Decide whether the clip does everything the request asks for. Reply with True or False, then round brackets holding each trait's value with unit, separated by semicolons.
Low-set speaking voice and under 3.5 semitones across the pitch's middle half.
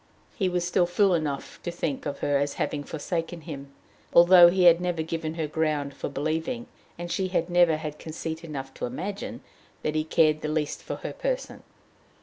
False (160 Hz; 2.7 semitones)